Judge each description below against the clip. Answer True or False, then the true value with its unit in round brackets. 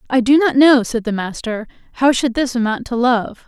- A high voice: True (245 Hz)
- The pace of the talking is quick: True (225 wpm)